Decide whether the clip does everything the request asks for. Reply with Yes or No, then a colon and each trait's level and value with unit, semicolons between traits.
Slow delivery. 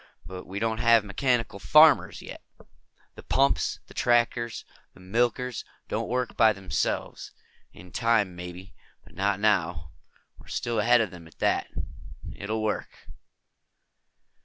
Yes: slow, 130 wpm